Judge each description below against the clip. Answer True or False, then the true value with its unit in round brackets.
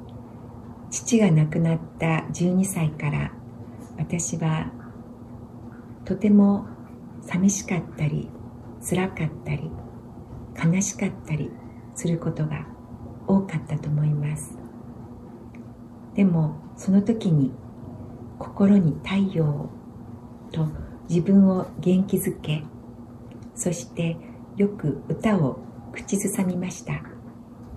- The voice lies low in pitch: False (145 Hz)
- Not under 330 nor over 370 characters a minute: False (170 characters per minute)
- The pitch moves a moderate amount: False (7.0 semitones)